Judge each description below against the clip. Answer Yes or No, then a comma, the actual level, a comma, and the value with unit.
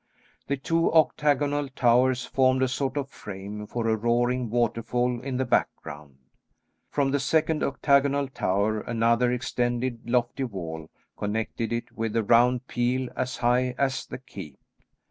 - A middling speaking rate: Yes, average, 145 wpm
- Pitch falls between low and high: No, low, 125 Hz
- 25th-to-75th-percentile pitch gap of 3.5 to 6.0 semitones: No, narrow, 2.5 semitones